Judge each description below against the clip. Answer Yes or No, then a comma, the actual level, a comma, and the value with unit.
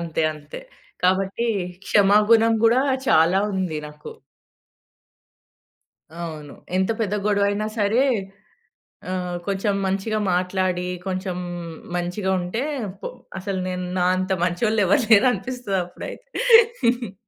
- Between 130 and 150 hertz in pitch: No, high, 190 Hz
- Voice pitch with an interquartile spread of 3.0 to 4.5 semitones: Yes, average, 3.3 semitones